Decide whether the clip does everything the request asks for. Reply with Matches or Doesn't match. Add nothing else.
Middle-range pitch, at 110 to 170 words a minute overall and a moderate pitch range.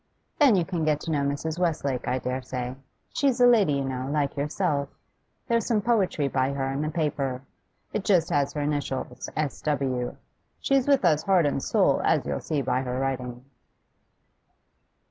Doesn't match